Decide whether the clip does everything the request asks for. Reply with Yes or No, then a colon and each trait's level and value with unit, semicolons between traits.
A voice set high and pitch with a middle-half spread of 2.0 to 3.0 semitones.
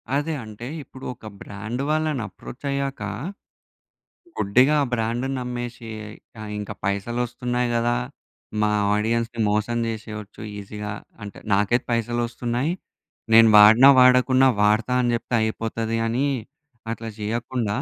No: low, 115 Hz; average, 2.7 semitones